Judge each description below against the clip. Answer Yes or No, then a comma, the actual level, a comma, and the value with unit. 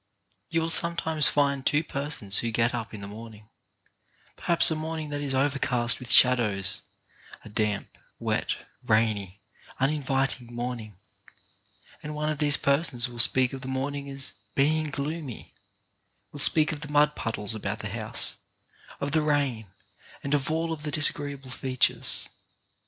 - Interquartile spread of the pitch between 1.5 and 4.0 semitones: No, average, 4.4 semitones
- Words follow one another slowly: No, average, 165 wpm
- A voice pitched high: No, low, 135 Hz